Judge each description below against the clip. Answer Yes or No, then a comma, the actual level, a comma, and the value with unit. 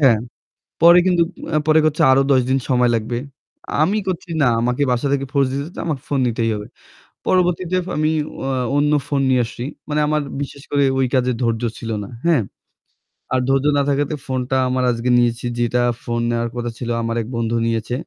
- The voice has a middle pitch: No, low, 130 Hz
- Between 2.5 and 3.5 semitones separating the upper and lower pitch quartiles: No, average, 3.9 semitones